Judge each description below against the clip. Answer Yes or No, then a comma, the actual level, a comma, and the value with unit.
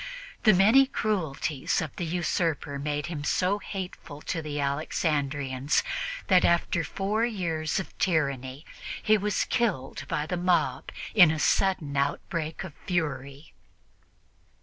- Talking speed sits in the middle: No, slow, 125 wpm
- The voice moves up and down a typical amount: Yes, average, 4.5 semitones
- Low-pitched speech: No, medium, 160 Hz